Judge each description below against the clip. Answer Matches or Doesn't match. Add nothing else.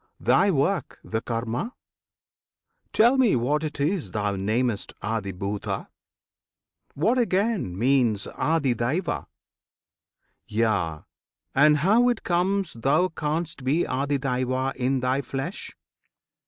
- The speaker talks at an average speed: Doesn't match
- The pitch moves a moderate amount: Doesn't match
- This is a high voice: Doesn't match